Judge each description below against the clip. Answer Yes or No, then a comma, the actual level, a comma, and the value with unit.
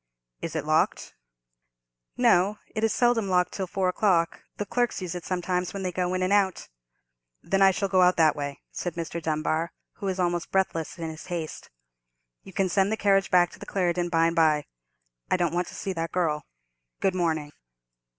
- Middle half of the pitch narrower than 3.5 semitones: Yes, narrow, 2.6 semitones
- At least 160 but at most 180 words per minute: No, average, 200 wpm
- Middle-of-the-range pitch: Yes, medium, 180 Hz